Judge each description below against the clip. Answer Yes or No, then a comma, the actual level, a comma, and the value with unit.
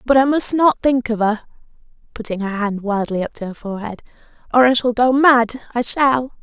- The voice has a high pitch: Yes, high, 235 Hz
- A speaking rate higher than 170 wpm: Yes, fast, 205 wpm